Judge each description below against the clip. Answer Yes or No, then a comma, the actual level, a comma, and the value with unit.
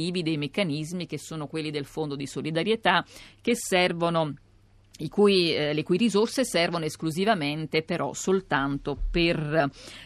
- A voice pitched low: No, medium, 160 Hz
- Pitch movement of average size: Yes, average, 3.6 semitones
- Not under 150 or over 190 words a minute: No, average, 130 wpm